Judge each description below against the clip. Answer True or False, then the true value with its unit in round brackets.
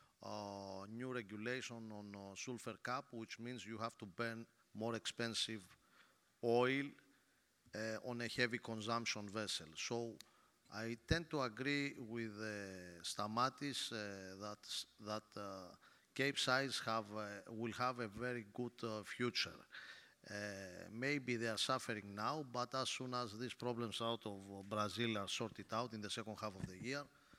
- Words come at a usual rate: True (150 wpm)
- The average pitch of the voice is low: True (115 Hz)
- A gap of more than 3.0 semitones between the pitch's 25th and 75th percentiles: False (2.7 semitones)